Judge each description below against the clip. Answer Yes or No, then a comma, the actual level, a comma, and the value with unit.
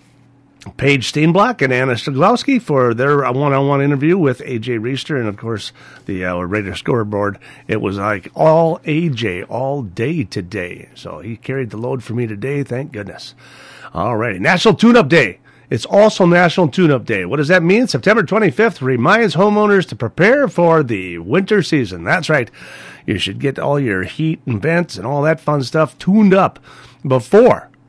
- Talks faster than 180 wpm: No, average, 175 wpm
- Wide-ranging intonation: Yes, wide, 6.8 semitones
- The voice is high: No, medium, 140 Hz